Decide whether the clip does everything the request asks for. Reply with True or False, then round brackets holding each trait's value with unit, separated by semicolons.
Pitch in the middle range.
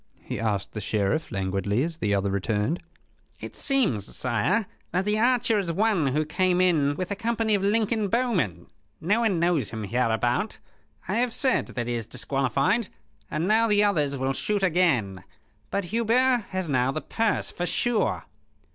True (170 Hz)